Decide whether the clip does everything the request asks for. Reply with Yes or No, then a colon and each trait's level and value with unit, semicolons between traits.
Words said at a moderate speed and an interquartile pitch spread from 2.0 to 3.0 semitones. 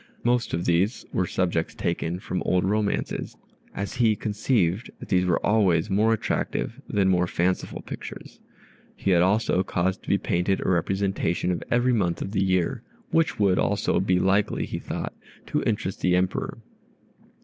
Yes: average, 165 wpm; narrow, 2.5 semitones